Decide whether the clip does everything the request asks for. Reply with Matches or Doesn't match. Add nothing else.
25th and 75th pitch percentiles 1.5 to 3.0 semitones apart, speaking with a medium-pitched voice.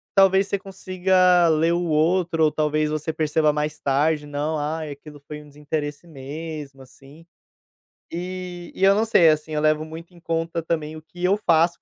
Matches